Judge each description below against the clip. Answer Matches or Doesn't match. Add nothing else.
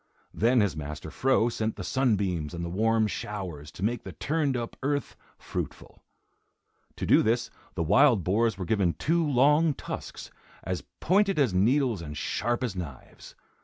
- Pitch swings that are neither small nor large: Doesn't match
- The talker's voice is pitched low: Matches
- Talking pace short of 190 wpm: Matches